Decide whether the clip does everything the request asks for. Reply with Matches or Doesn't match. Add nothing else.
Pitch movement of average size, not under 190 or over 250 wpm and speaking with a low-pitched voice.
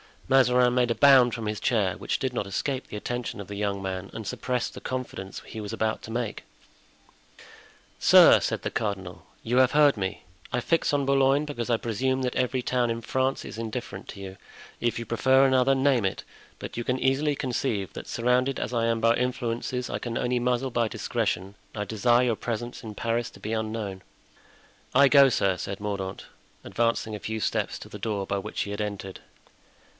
Matches